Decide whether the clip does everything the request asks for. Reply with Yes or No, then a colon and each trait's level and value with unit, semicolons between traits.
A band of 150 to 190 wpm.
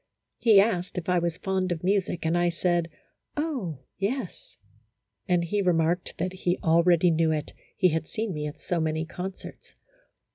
Yes: average, 170 wpm